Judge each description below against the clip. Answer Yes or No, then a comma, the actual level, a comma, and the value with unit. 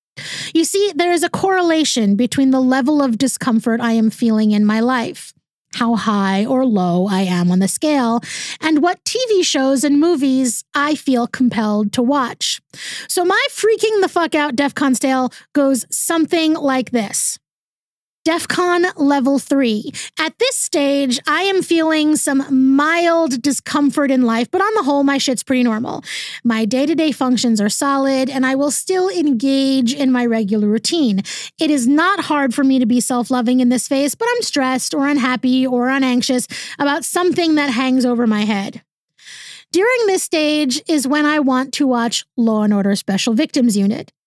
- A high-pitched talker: Yes, very high, 270 Hz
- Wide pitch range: No, average, 4.4 semitones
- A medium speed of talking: Yes, average, 170 wpm